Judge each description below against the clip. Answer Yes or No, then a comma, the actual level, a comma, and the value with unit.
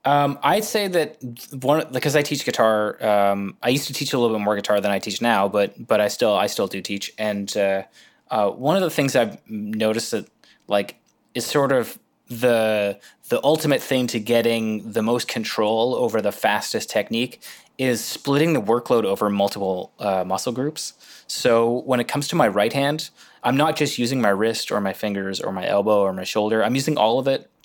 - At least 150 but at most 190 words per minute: No, fast, 205 wpm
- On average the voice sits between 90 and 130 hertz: Yes, low, 115 Hz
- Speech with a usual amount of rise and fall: Yes, average, 4.9 semitones